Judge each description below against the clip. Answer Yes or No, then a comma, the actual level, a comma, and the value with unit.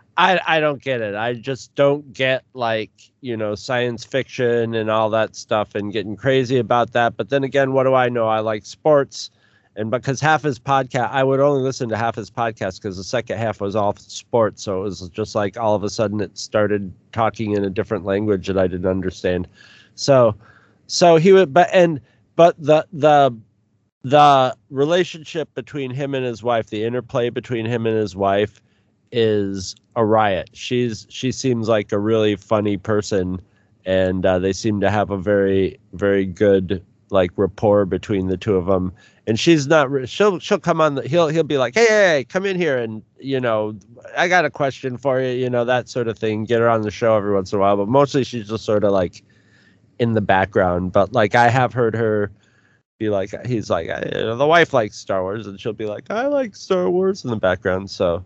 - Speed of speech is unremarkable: No, fast, 215 wpm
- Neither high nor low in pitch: No, low, 110 Hz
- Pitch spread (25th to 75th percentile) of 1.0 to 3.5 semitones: No, average, 4.3 semitones